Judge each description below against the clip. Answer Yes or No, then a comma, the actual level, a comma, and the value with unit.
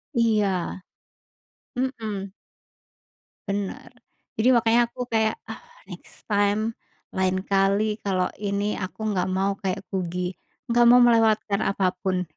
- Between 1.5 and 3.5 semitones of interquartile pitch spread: Yes, average, 2.8 semitones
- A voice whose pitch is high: Yes, high, 200 Hz